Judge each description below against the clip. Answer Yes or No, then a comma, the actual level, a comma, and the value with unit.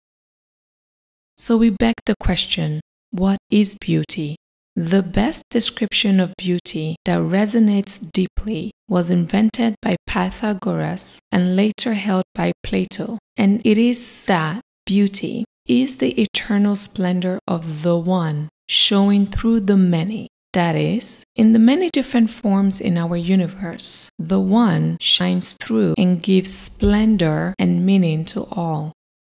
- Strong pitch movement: No, average, 3.5 semitones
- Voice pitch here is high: Yes, high, 195 Hz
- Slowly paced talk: Yes, slow, 125 wpm